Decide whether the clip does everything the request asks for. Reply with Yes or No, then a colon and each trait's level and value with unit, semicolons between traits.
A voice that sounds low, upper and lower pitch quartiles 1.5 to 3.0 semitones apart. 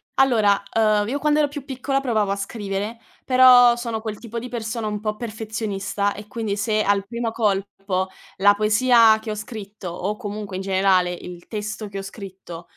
No: high, 215 Hz; average, 2.7 semitones